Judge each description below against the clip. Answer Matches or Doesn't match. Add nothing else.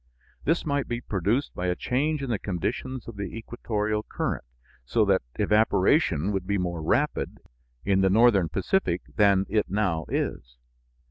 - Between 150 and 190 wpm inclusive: Matches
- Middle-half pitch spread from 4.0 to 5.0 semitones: Matches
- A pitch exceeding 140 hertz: Doesn't match